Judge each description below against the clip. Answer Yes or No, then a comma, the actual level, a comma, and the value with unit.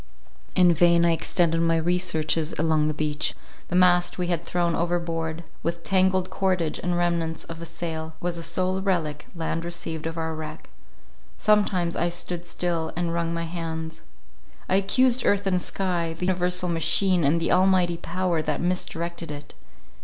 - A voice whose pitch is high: No, medium, 170 Hz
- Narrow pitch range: Yes, narrow, 1.7 semitones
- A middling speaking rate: Yes, average, 165 wpm